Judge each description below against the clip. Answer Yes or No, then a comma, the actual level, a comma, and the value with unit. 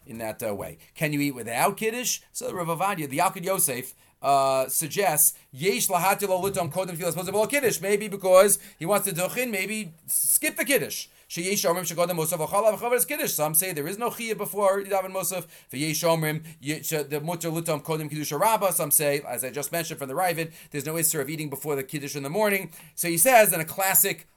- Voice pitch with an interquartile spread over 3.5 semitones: Yes, average, 4.5 semitones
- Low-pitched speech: No, medium, 175 Hz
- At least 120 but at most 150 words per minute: No, average, 165 wpm